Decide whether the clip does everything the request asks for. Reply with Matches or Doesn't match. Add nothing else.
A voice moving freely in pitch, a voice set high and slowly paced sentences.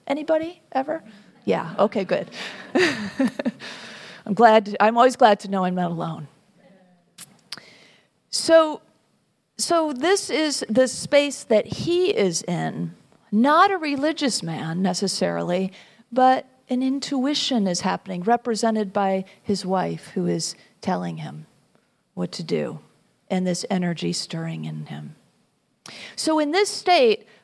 Matches